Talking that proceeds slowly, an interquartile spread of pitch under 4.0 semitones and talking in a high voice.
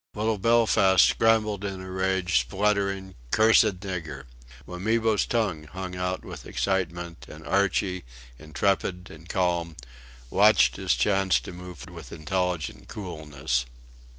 No: slow, 120 wpm; average, 2.8 semitones; very low, 95 Hz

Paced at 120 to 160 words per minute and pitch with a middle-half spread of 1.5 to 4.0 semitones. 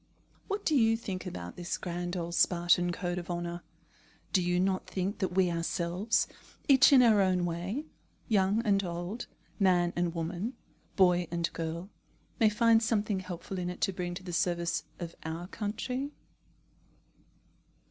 Yes: average, 155 wpm; average, 3.0 semitones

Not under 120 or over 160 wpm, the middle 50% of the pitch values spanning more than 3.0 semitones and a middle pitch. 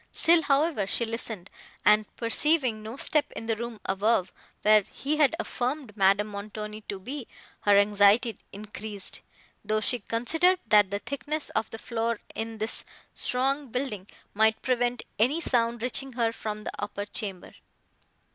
No: average, 150 wpm; average, 3.6 semitones; high, 225 Hz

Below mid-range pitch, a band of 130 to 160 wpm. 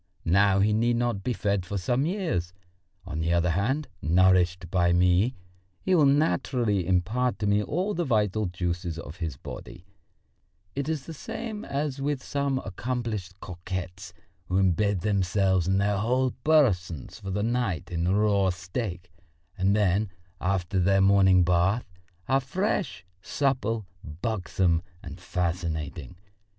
Yes: very low, 95 Hz; average, 140 wpm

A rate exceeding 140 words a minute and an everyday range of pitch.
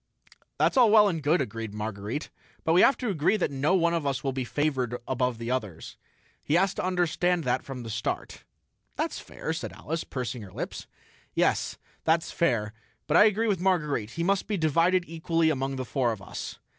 No: average, 195 wpm; wide, 6.0 semitones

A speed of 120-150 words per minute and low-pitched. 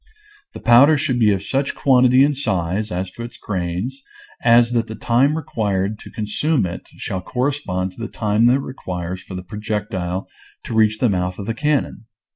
No: average, 190 wpm; low, 110 Hz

